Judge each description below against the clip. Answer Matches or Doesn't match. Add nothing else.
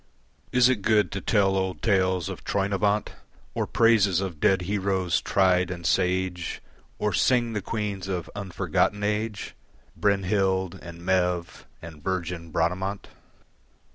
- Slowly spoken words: Matches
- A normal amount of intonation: Doesn't match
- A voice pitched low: Matches